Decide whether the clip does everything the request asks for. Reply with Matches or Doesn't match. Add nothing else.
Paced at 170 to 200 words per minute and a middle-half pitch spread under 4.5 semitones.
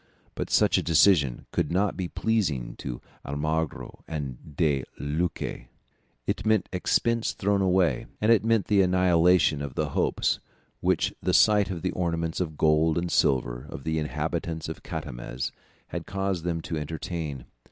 Doesn't match